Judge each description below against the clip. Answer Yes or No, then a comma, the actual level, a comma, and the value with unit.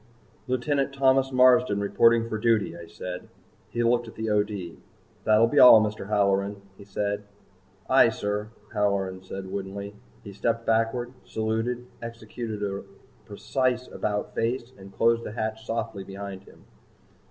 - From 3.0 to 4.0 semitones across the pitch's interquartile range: No, narrow, 2.6 semitones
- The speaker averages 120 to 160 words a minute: Yes, average, 140 wpm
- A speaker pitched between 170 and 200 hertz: No, low, 110 Hz